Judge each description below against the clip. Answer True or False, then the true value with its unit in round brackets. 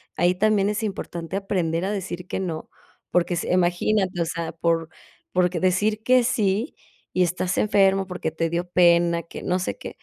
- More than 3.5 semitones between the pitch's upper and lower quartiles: False (2.5 semitones)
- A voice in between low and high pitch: True (180 Hz)